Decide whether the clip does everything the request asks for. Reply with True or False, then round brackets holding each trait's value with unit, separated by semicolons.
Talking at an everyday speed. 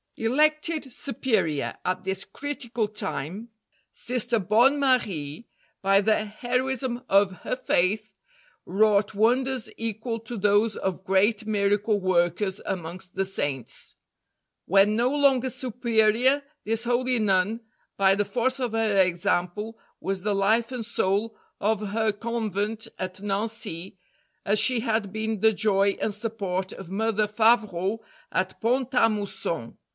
False (130 wpm)